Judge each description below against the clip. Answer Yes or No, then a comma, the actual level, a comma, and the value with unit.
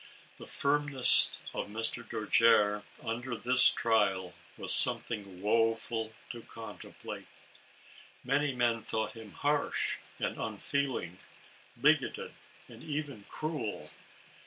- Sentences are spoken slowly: Yes, slow, 100 wpm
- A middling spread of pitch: Yes, average, 3.7 semitones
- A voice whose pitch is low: Yes, low, 115 Hz